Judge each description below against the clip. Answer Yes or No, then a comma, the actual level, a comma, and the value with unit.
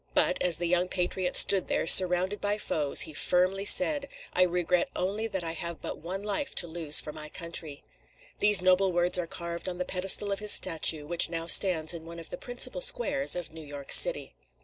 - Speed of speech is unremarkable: No, fast, 210 wpm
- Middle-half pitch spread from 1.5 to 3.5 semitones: Yes, average, 2.8 semitones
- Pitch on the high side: No, medium, 180 Hz